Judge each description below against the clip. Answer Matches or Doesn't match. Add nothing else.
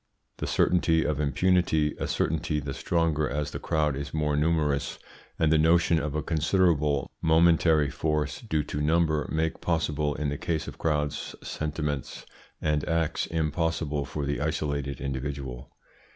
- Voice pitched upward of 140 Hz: Doesn't match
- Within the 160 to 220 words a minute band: Doesn't match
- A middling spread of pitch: Doesn't match